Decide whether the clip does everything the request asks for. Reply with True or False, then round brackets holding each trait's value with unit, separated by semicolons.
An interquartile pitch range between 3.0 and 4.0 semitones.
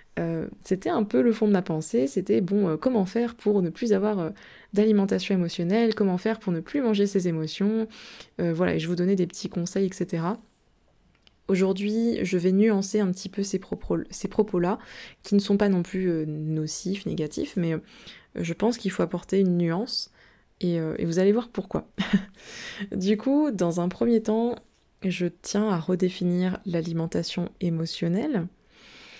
True (3.3 semitones)